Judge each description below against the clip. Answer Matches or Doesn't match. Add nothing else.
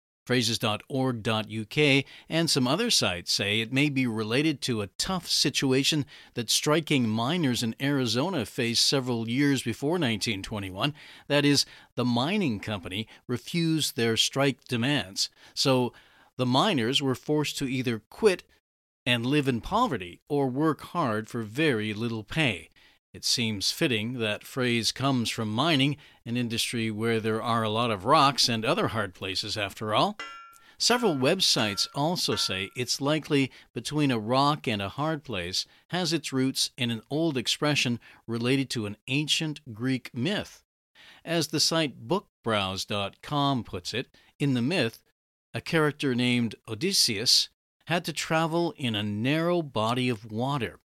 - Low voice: Matches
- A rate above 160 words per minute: Doesn't match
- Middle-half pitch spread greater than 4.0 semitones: Matches